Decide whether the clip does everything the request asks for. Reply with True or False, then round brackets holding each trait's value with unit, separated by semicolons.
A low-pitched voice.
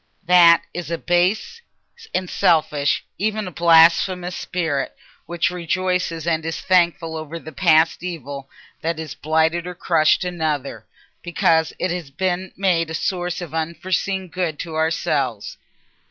False (170 Hz)